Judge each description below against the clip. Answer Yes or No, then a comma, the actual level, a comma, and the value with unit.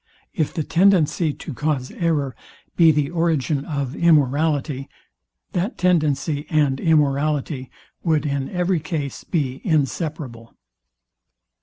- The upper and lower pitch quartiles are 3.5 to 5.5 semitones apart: No, average, 2.9 semitones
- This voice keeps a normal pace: No, slow, 110 wpm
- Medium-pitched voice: Yes, medium, 150 Hz